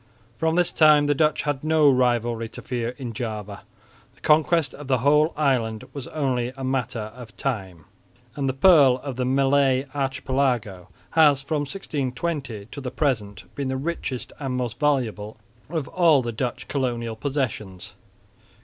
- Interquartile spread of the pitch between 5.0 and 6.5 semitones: No, average, 3.7 semitones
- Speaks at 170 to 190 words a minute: No, average, 160 wpm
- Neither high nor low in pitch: No, low, 130 Hz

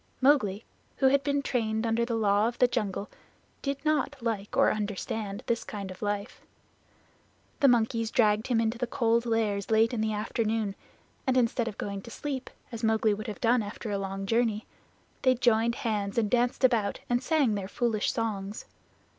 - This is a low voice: No, high, 225 Hz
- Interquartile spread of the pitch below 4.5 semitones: Yes, average, 2.7 semitones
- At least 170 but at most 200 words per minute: Yes, average, 180 wpm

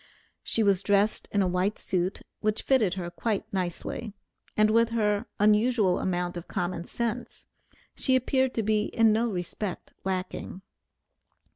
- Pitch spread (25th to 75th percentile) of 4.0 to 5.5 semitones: No, average, 3.5 semitones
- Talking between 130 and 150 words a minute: Yes, average, 145 wpm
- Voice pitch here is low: No, high, 210 Hz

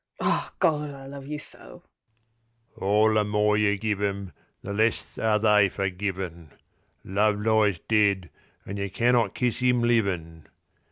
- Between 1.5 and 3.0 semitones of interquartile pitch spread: Yes, narrow, 2.5 semitones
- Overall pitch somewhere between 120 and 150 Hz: No, low, 105 Hz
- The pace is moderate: Yes, average, 145 wpm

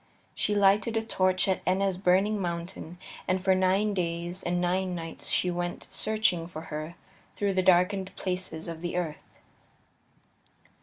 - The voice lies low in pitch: No, medium, 185 Hz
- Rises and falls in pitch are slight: Yes, narrow, 1.8 semitones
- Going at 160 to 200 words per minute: No, average, 150 wpm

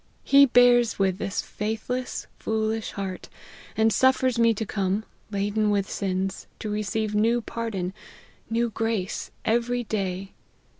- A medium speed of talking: No, slow, 130 wpm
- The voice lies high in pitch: Yes, high, 220 Hz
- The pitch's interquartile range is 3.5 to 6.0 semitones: No, average, 2.8 semitones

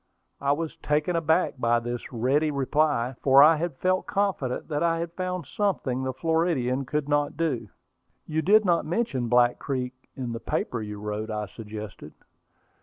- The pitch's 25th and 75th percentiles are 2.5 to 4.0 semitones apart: No, average, 5.2 semitones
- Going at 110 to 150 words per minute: No, average, 170 wpm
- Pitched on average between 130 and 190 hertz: Yes, medium, 140 Hz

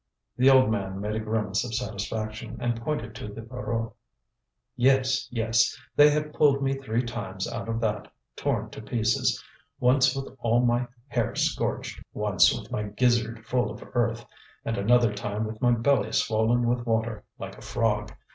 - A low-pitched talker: Yes, low, 115 Hz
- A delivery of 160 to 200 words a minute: Yes, average, 170 wpm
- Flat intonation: Yes, narrow, 2.3 semitones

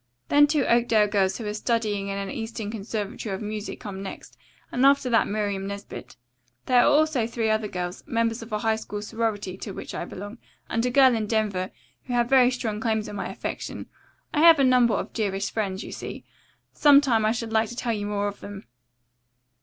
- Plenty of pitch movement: No, average, 2.8 semitones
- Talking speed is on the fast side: Yes, fast, 210 wpm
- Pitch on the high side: Yes, high, 220 Hz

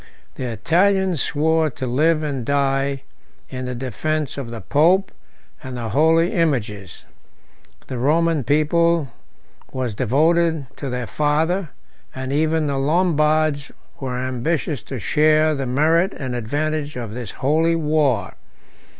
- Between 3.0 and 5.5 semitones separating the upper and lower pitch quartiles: Yes, average, 3.8 semitones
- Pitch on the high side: No, medium, 145 Hz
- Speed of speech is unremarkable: No, slow, 130 wpm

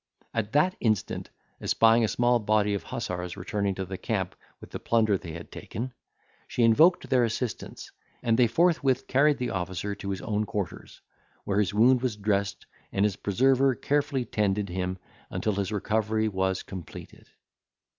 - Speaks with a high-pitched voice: No, low, 105 Hz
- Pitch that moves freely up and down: No, average, 3.8 semitones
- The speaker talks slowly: No, average, 165 wpm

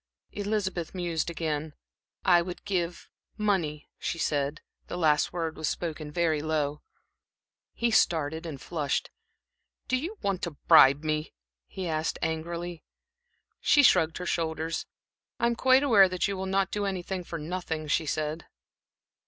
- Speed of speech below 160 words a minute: Yes, average, 145 wpm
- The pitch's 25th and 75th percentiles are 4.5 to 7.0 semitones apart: No, average, 3.3 semitones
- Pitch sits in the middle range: Yes, medium, 170 Hz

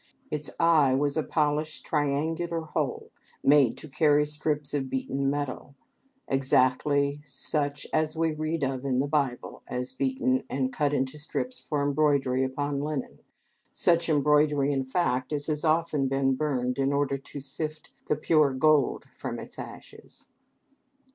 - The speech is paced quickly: No, average, 150 wpm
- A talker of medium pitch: Yes, medium, 145 Hz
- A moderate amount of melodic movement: No, narrow, 2.2 semitones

